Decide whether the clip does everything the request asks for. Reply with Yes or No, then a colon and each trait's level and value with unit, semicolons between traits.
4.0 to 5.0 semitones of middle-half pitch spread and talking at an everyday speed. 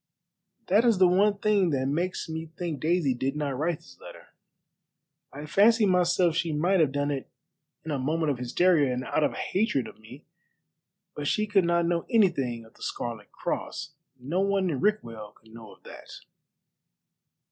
No: wide, 5.5 semitones; average, 180 wpm